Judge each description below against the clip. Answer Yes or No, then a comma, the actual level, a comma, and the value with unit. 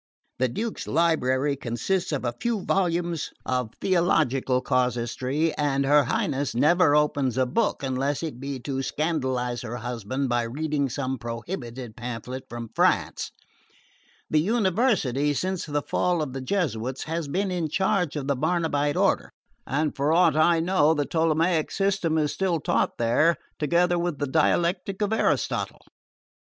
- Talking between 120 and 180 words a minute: Yes, average, 150 wpm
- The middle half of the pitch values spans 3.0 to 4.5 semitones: No, average, 4.9 semitones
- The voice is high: No, medium, 145 Hz